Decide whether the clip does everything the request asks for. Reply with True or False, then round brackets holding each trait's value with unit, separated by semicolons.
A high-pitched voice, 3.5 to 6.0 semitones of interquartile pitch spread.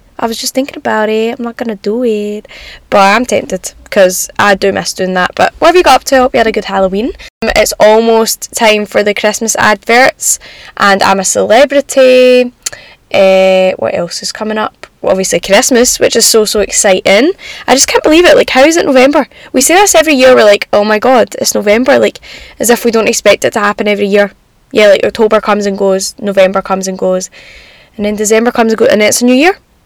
True (220 Hz; 4.1 semitones)